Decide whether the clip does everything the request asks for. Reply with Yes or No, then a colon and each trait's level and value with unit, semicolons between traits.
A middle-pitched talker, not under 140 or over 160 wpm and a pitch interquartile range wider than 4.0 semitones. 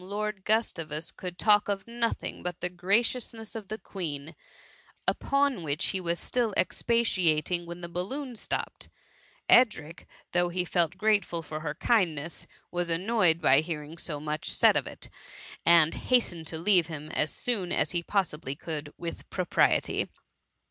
Yes: medium, 175 Hz; average, 150 wpm; average, 4.6 semitones